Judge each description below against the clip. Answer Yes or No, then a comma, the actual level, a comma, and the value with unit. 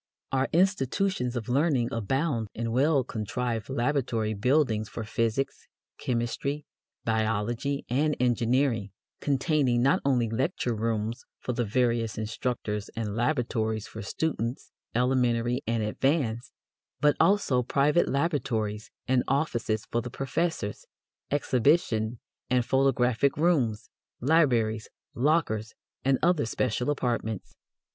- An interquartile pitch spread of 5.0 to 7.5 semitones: No, average, 3.6 semitones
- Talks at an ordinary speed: No, slow, 110 wpm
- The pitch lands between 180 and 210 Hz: No, low, 125 Hz